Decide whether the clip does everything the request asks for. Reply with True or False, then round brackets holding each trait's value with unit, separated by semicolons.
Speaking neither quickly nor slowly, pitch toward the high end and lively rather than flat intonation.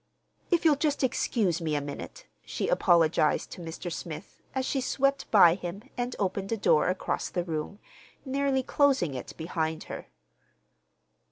True (155 wpm; 195 Hz; 8.4 semitones)